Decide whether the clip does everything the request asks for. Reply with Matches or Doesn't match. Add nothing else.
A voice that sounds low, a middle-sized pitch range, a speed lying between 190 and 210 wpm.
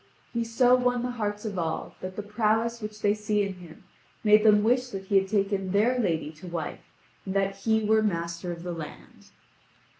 Doesn't match